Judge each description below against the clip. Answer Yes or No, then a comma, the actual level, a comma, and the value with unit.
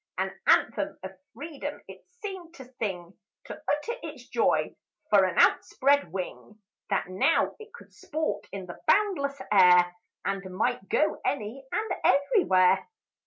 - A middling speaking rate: Yes, average, 145 wpm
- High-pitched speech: Yes, very high, 255 Hz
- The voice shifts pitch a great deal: Yes, wide, 8.5 semitones